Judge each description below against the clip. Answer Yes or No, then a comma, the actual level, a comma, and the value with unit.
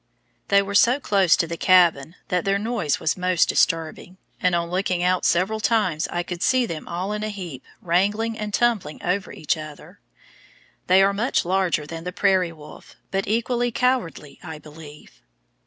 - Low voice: No, medium, 185 Hz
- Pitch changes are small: No, average, 3.7 semitones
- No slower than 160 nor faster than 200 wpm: Yes, average, 175 wpm